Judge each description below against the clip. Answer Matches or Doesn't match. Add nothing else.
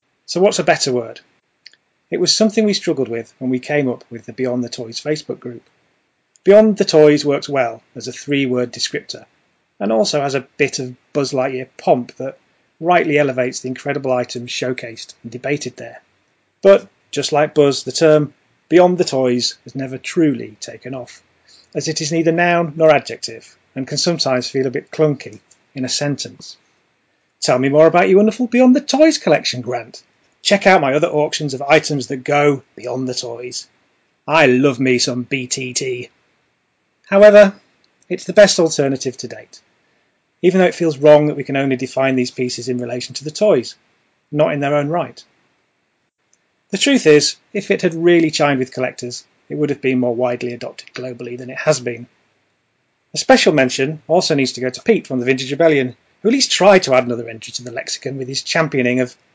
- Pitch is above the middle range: Doesn't match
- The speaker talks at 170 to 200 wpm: Matches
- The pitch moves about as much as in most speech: Matches